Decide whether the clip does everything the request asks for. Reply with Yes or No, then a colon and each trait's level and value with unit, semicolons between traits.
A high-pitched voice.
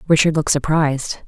No: medium, 150 Hz